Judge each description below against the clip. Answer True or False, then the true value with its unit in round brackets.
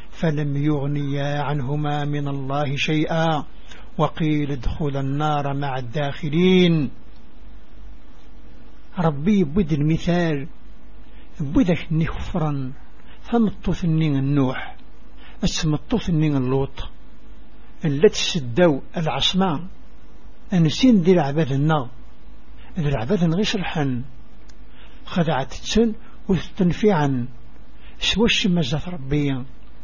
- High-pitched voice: False (155 Hz)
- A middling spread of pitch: True (4.1 semitones)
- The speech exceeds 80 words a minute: False (75 wpm)